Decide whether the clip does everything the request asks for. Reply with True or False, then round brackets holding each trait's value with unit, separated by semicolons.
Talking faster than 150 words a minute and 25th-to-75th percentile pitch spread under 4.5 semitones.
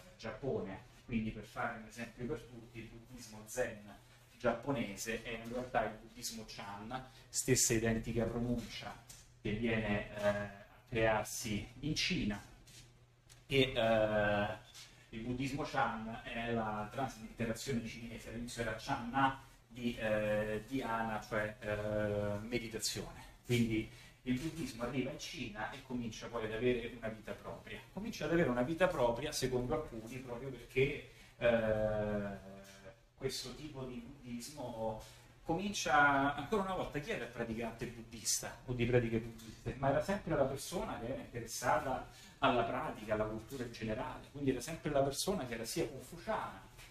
False (145 wpm; 2.6 semitones)